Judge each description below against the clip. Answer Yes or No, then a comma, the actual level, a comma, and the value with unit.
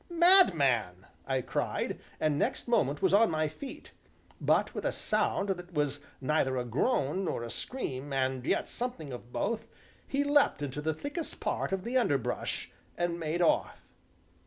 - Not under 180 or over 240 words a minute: No, average, 160 wpm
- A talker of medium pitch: Yes, medium, 155 Hz